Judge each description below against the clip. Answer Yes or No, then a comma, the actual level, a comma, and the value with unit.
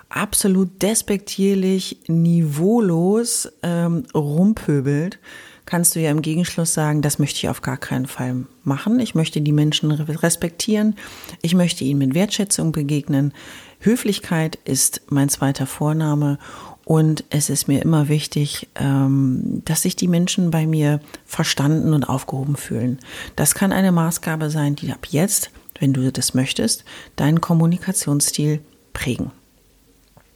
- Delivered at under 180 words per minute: Yes, average, 130 wpm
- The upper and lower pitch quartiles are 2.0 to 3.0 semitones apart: No, average, 3.9 semitones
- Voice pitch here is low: No, medium, 155 Hz